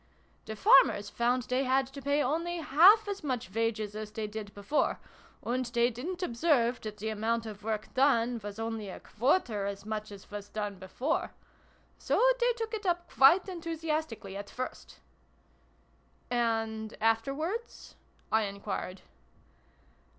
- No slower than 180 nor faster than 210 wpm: No, average, 155 wpm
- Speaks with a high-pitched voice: Yes, high, 235 Hz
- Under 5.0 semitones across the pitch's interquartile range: No, wide, 5.6 semitones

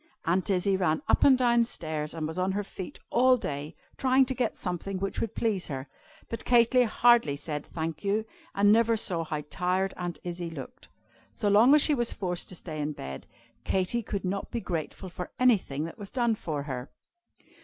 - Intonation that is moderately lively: No, wide, 6.1 semitones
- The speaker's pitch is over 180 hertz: Yes, high, 190 Hz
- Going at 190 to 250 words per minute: Yes, average, 195 wpm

